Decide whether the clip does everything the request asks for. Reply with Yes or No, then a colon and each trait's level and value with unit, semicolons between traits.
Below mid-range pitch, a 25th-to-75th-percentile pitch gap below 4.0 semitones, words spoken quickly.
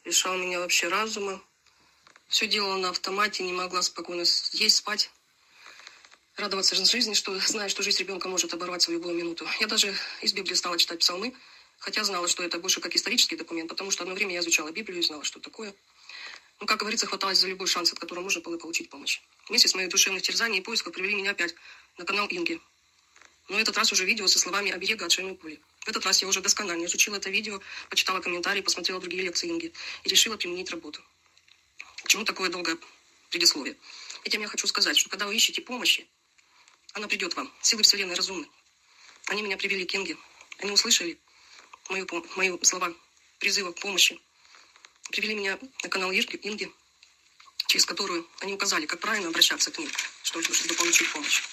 No: high, 195 Hz; average, 2.9 semitones; fast, 185 wpm